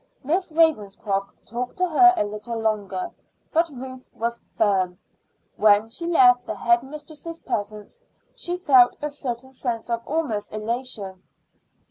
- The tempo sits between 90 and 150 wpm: Yes, slow, 135 wpm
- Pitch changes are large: Yes, wide, 5.9 semitones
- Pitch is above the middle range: Yes, high, 240 Hz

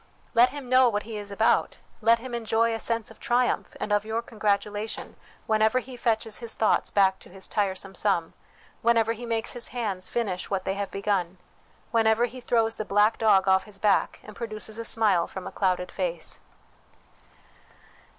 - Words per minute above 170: Yes, average, 180 wpm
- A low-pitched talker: No, high, 220 Hz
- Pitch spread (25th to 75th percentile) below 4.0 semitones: Yes, narrow, 2.6 semitones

